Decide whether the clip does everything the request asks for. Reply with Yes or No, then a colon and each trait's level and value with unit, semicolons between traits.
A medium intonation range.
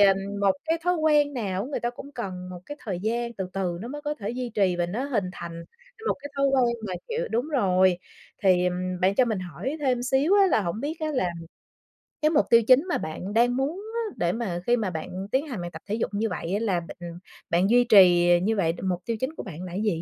No: wide, 6.5 semitones